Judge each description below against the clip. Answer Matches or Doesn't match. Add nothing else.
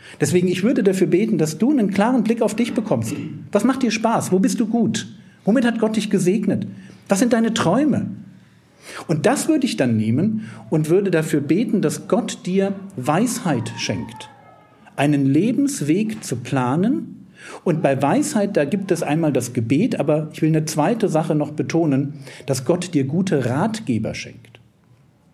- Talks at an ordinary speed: Matches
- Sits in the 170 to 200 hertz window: Matches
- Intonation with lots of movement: Matches